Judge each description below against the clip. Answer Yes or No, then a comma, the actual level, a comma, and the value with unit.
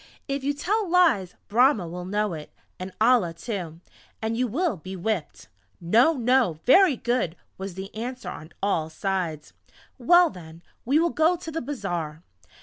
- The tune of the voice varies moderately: No, wide, 7.6 semitones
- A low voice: No, high, 220 Hz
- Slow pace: No, average, 160 wpm